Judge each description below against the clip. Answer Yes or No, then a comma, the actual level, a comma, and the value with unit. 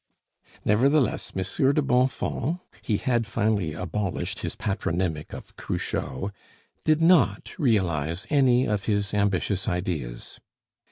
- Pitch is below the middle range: Yes, low, 105 Hz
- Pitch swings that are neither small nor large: No, wide, 5.9 semitones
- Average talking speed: No, slow, 110 wpm